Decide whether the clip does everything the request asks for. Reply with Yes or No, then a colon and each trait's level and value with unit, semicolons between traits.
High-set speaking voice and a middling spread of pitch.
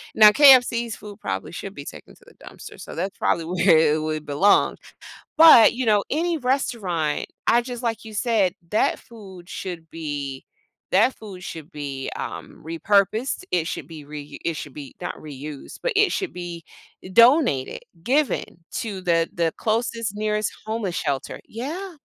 No: high, 195 Hz; wide, 6.6 semitones